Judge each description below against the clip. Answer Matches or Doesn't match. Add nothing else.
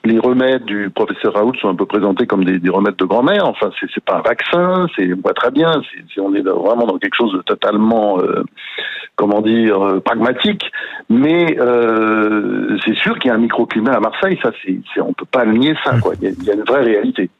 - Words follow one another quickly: Matches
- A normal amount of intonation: Matches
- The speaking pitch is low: Matches